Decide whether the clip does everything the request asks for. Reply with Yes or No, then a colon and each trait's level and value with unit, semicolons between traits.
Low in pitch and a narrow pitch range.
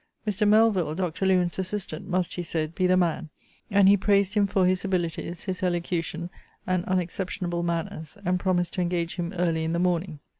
No: medium, 180 Hz; narrow, 1.8 semitones